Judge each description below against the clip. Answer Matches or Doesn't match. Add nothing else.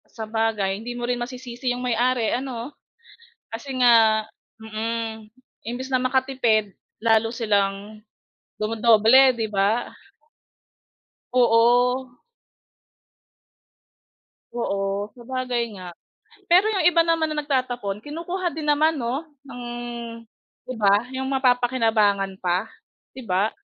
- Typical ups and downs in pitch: Matches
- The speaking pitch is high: Matches